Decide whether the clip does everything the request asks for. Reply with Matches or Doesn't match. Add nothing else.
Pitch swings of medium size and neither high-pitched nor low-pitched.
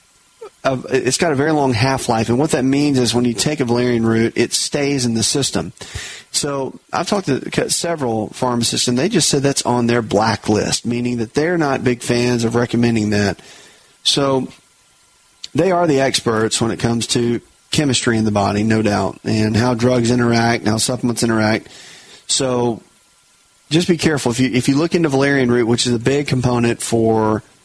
Doesn't match